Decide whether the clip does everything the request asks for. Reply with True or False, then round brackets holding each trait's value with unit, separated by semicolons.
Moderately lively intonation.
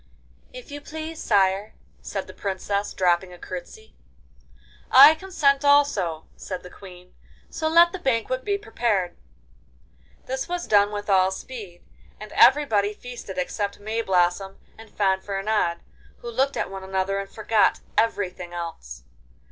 False (6.0 semitones)